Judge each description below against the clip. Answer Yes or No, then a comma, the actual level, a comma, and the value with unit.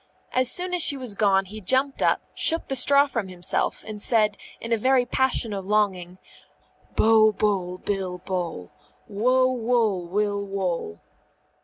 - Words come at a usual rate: Yes, average, 155 wpm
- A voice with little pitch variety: No, average, 4.8 semitones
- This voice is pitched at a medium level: No, high, 210 Hz